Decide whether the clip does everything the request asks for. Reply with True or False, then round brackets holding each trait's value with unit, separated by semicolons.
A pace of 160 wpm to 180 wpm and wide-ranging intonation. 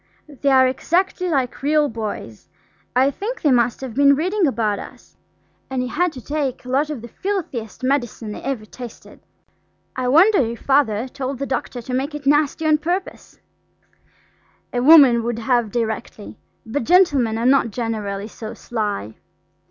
False (165 wpm; 4.2 semitones)